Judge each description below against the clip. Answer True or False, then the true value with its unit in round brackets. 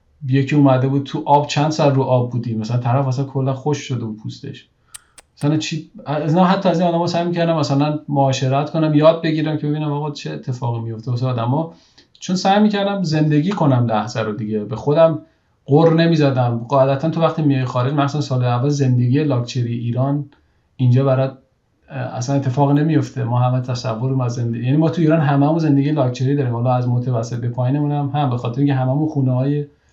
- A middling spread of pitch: True (3.2 semitones)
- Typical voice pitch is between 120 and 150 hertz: True (140 Hz)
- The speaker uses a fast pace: True (185 wpm)